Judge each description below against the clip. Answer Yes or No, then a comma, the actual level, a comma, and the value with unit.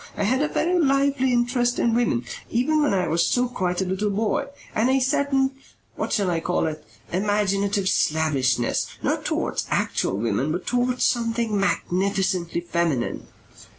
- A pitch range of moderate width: No, wide, 6.4 semitones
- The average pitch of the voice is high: Yes, high, 205 Hz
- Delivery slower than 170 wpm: Yes, average, 155 wpm